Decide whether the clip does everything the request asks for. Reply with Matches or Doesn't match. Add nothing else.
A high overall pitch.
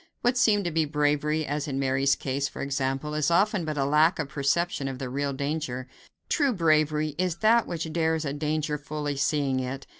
Doesn't match